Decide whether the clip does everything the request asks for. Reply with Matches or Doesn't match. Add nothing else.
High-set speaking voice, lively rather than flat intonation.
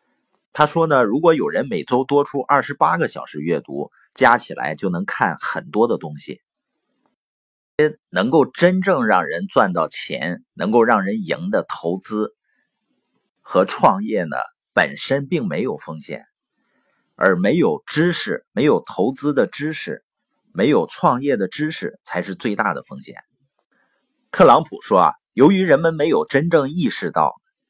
Doesn't match